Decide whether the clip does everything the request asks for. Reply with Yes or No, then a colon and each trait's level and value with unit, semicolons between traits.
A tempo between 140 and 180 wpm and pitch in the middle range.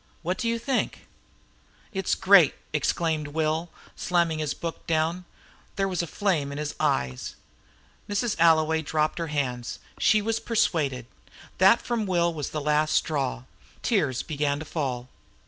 Yes: average, 155 wpm; medium, 160 Hz